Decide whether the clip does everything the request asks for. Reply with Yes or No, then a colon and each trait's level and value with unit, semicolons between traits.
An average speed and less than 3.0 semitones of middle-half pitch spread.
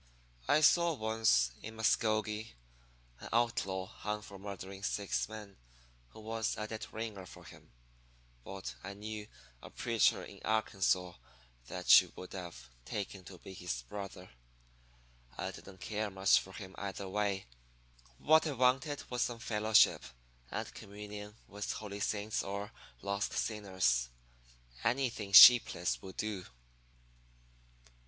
No: slow, 130 wpm; narrow, 2.5 semitones